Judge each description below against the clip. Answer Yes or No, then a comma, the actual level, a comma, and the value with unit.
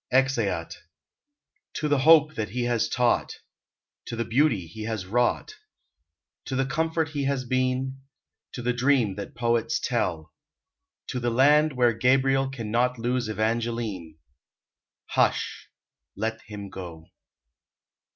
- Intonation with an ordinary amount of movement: Yes, average, 3.4 semitones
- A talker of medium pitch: No, low, 120 Hz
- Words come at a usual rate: No, slow, 130 wpm